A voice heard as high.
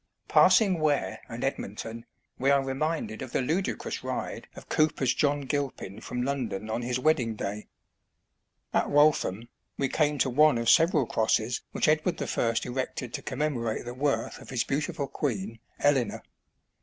No: low, 130 Hz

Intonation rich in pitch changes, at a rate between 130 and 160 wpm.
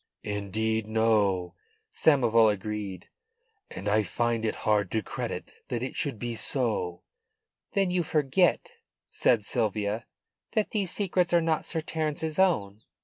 Yes: wide, 7.1 semitones; slow, 135 wpm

